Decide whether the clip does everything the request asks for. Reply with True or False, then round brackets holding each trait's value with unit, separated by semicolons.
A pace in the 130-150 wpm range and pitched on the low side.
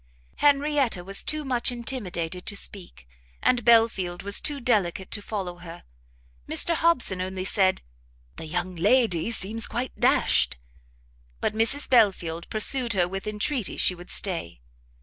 False (140 wpm; 205 Hz)